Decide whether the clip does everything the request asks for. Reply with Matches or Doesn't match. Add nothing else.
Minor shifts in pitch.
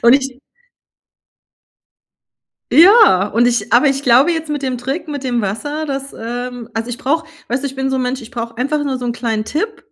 Doesn't match